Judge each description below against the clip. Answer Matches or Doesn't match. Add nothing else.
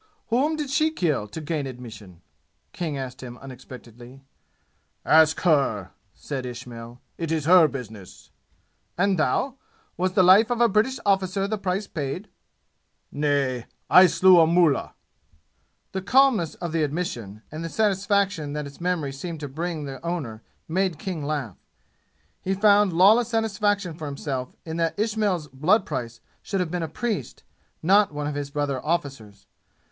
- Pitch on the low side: Doesn't match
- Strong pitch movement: Matches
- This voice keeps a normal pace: Matches